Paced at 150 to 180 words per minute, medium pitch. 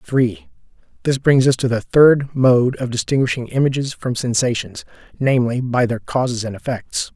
No: average, 160 wpm; low, 125 Hz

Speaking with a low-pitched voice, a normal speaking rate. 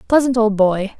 No: high, 220 Hz; average, 180 wpm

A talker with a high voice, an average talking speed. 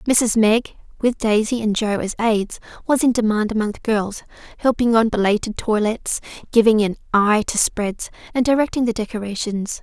Yes: high, 220 Hz; average, 165 wpm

